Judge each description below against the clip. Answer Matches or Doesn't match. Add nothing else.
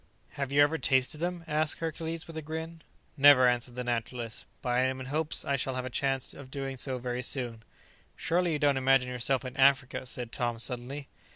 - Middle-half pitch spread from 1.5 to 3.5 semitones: Matches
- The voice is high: Doesn't match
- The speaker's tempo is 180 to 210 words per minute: Matches